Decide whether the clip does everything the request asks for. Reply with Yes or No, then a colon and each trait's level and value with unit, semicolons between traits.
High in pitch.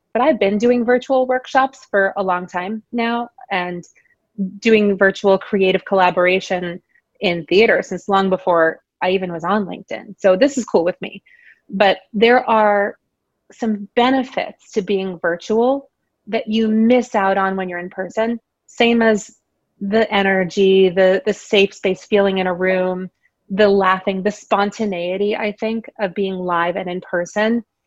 Yes: high, 200 Hz